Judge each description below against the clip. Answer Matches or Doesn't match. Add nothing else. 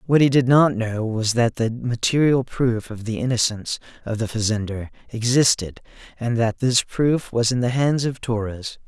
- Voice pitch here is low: Matches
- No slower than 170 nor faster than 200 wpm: Matches